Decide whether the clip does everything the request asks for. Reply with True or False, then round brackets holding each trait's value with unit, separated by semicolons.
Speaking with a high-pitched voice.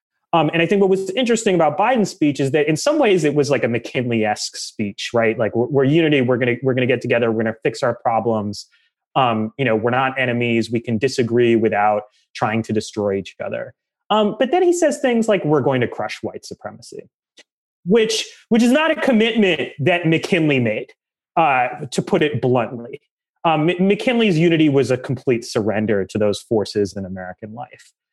False (135 Hz)